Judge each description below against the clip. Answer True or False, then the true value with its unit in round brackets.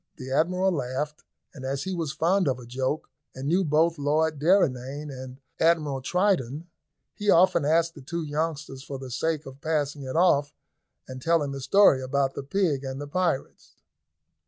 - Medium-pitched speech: True (145 Hz)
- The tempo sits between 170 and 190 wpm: True (175 wpm)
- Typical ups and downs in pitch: True (3.8 semitones)